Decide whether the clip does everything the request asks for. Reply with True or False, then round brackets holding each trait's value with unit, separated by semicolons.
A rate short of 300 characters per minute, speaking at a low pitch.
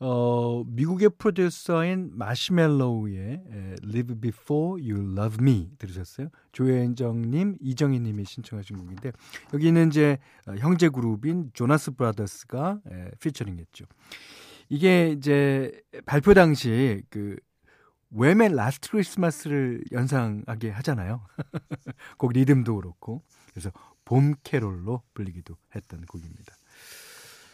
True (290 characters per minute; 130 Hz)